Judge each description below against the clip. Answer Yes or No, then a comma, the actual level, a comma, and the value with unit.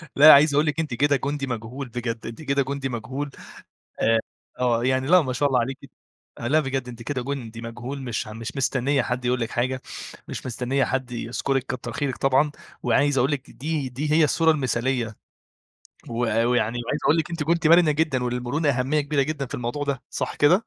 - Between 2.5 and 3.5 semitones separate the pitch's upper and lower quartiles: Yes, average, 3.0 semitones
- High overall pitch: No, low, 130 Hz